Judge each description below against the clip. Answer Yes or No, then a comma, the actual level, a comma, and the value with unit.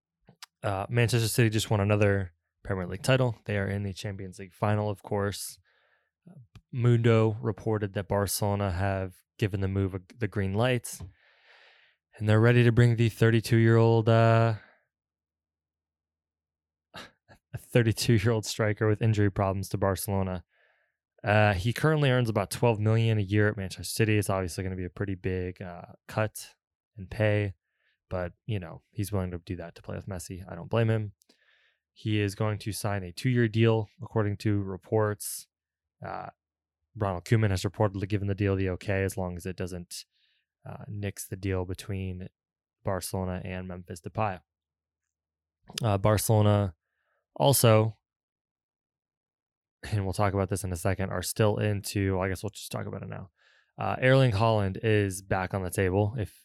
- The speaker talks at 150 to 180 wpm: Yes, average, 165 wpm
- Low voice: Yes, low, 100 Hz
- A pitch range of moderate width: Yes, average, 3.0 semitones